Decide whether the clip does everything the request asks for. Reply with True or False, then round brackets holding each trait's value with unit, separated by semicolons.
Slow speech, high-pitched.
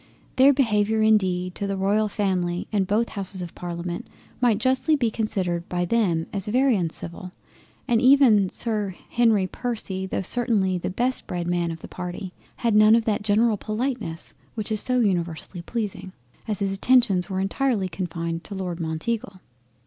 False (165 wpm; 200 Hz)